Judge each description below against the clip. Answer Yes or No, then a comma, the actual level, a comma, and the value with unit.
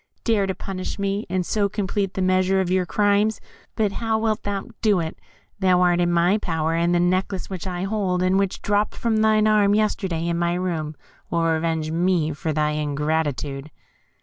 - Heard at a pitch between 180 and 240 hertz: Yes, medium, 185 Hz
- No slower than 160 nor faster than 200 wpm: Yes, average, 190 wpm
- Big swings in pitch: No, average, 3.3 semitones